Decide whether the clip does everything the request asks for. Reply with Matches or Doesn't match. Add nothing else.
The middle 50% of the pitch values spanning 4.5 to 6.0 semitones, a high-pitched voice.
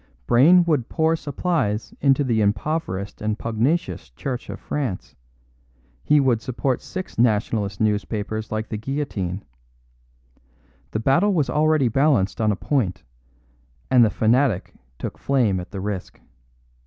Doesn't match